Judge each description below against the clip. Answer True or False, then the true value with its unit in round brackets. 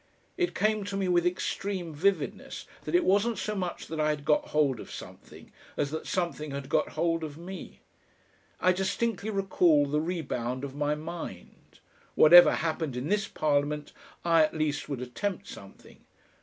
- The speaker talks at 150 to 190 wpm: True (170 wpm)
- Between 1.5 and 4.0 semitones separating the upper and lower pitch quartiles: False (4.5 semitones)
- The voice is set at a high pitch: False (165 Hz)